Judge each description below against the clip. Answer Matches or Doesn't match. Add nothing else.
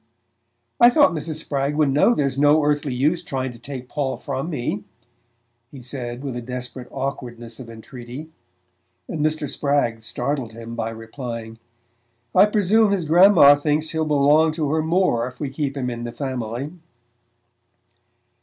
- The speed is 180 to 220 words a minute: Doesn't match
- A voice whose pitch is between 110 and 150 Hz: Matches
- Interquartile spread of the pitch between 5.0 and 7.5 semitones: Doesn't match